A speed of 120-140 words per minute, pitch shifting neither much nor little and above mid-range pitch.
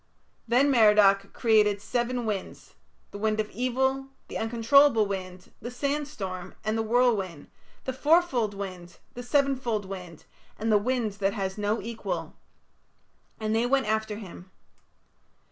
Yes: slow, 135 wpm; average, 3.8 semitones; high, 220 Hz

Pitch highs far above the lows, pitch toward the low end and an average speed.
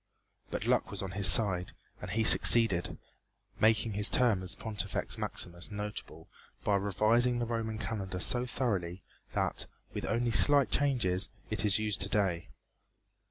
No: average, 3.3 semitones; low, 105 Hz; average, 150 wpm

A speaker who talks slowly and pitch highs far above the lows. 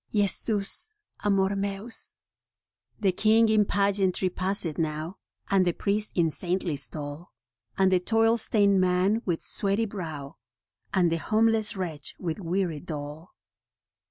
No: slow, 130 wpm; average, 3.4 semitones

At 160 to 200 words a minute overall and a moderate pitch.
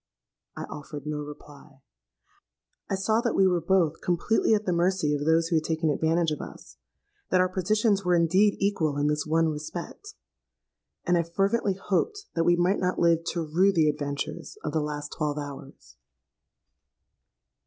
Yes: average, 165 wpm; medium, 165 Hz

